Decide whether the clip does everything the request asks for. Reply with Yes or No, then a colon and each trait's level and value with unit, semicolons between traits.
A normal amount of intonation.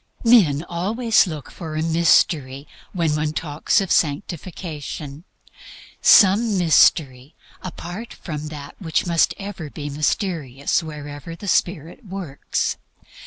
Yes: average, 3.9 semitones